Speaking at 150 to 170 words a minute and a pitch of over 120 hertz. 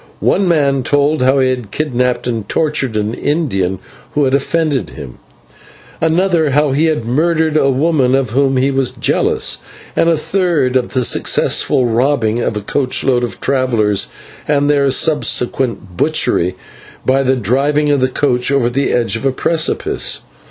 Yes: average, 165 wpm; low, 135 Hz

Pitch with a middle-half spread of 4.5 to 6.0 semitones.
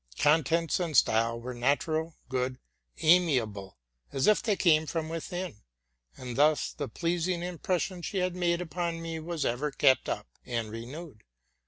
Yes: average, 5.2 semitones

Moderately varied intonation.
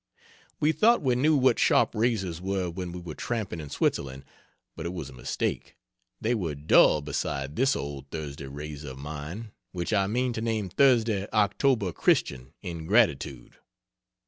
No: wide, 7.7 semitones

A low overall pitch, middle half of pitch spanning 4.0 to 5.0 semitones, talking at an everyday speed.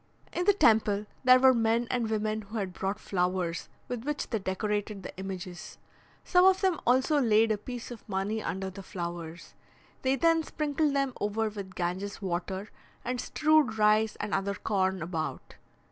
No: high, 215 Hz; average, 4.7 semitones; average, 170 wpm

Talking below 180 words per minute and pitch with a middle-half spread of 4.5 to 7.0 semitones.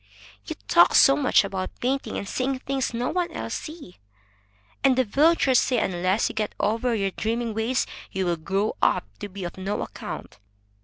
No: average, 185 wpm; average, 5.2 semitones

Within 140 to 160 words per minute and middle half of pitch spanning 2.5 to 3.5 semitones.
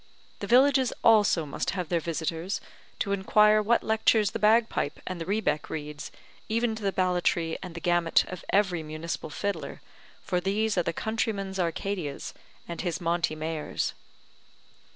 No: average, 150 wpm; average, 4.3 semitones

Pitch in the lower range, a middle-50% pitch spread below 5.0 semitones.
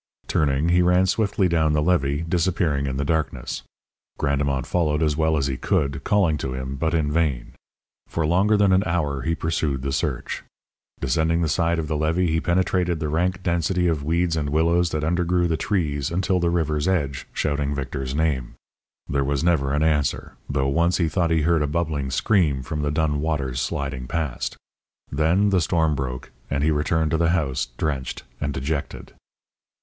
Yes: very low, 80 Hz; average, 3.2 semitones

